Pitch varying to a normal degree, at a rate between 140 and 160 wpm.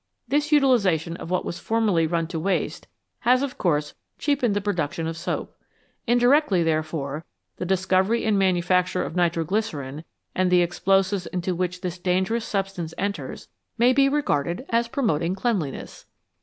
Yes: average, 5.0 semitones; average, 155 wpm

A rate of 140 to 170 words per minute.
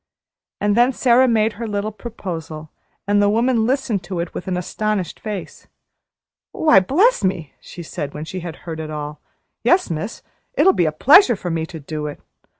No: average, 185 wpm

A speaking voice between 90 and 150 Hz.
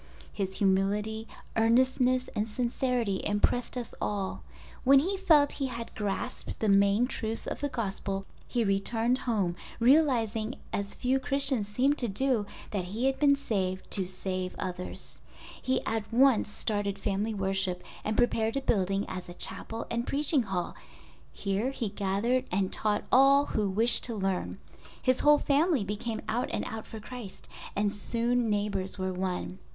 No: high, 220 Hz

